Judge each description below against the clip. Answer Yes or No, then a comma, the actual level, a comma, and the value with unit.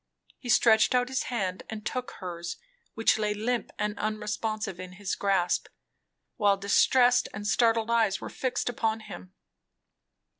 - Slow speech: No, average, 145 wpm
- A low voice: No, high, 215 Hz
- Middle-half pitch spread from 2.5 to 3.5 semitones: Yes, average, 2.8 semitones